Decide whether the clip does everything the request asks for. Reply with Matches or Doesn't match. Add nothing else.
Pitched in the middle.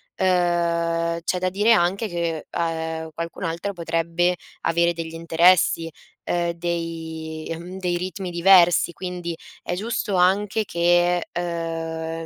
Matches